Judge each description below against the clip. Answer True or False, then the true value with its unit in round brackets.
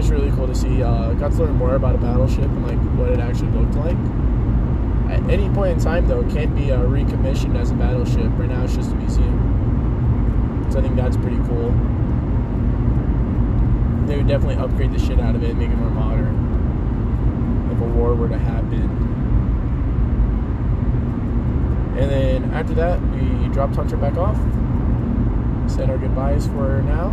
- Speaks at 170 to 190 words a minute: True (175 wpm)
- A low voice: True (65 Hz)